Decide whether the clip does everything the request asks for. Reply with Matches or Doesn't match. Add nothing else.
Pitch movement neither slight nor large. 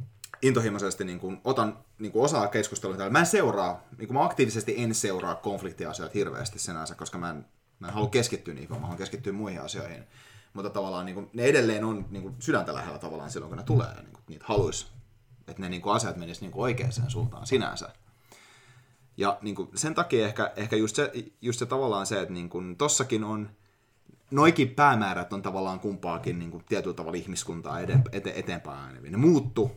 Matches